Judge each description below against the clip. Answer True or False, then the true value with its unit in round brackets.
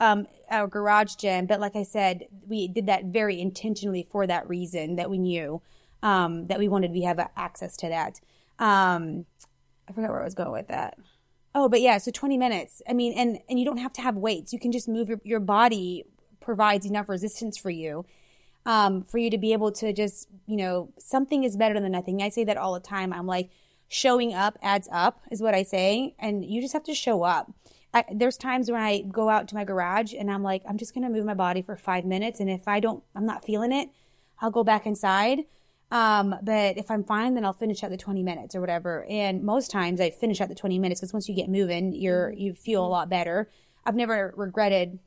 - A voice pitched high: True (205 Hz)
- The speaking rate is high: True (230 wpm)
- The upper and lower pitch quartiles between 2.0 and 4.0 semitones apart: True (3.1 semitones)